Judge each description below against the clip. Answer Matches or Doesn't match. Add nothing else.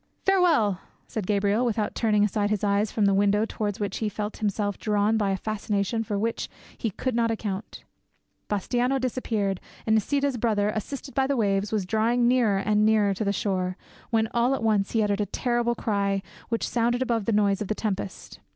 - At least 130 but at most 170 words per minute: Doesn't match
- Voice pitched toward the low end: Doesn't match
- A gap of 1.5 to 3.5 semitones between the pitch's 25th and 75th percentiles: Matches